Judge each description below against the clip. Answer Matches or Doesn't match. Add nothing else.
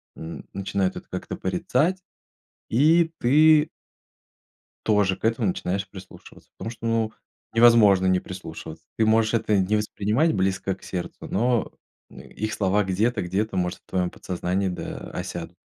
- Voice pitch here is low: Matches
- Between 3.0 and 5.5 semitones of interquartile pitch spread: Matches